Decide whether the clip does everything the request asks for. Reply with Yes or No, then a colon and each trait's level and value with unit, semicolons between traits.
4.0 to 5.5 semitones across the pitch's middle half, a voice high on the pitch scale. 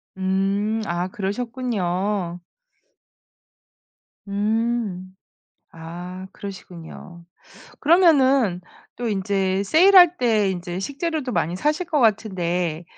Yes: average, 5.2 semitones; high, 200 Hz